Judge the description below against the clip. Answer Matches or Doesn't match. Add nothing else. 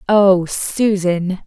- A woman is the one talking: Matches